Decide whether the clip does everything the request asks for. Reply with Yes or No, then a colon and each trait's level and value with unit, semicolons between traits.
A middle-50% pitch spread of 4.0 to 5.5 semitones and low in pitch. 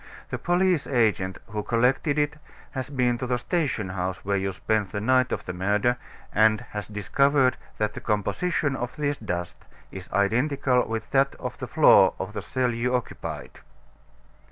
Yes: average, 4.7 semitones; low, 120 Hz